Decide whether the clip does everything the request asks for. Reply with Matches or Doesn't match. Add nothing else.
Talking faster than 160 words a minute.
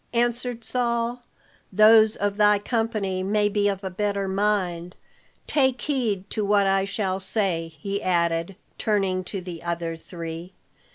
Doesn't match